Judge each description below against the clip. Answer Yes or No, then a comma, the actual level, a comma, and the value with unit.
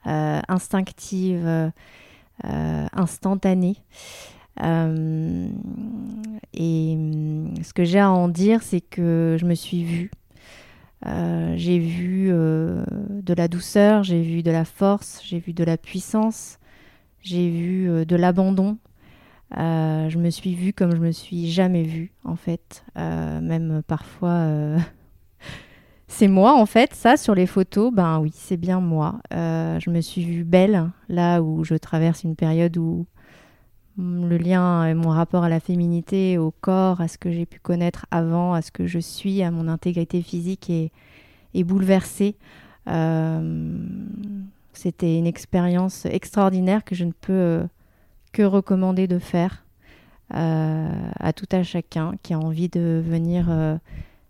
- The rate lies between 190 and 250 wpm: No, average, 150 wpm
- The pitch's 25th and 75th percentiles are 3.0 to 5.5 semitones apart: No, narrow, 2.5 semitones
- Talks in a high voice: No, medium, 175 Hz